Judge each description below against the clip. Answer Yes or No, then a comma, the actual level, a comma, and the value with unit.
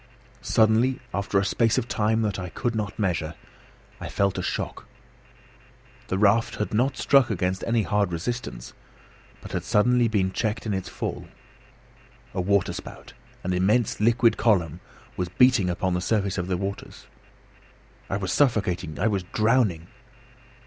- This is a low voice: Yes, low, 100 Hz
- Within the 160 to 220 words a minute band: No, average, 150 wpm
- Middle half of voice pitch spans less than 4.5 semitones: Yes, average, 3.7 semitones